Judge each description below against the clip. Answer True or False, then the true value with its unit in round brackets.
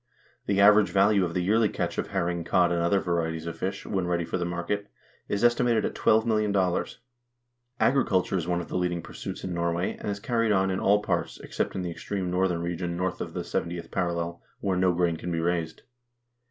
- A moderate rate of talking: False (210 wpm)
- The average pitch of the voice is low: True (90 Hz)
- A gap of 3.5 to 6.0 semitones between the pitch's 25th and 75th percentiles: False (2.7 semitones)